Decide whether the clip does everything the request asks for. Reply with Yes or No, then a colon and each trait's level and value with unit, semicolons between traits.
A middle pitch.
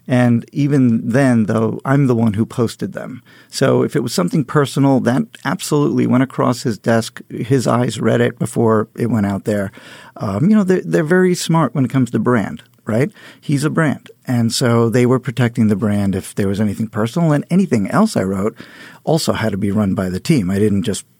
No: low, 120 Hz